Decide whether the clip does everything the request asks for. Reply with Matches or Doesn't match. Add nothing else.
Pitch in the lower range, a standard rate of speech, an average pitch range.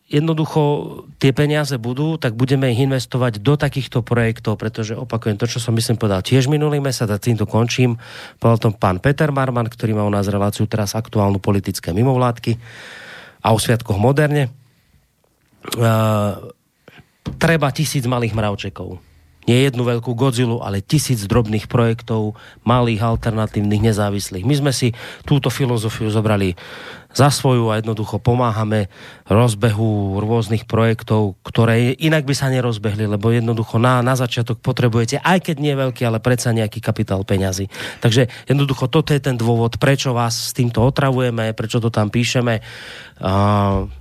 Matches